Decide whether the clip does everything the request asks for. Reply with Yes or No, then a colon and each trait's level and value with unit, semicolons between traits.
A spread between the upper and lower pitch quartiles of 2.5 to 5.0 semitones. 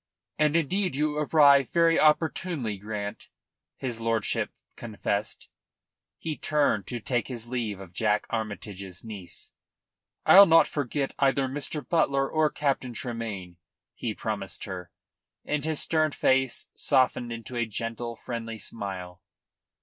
No: wide, 5.5 semitones